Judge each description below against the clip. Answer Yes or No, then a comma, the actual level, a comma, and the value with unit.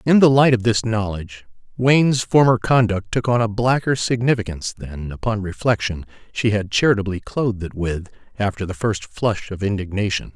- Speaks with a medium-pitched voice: No, low, 110 Hz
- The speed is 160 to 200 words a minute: Yes, average, 170 wpm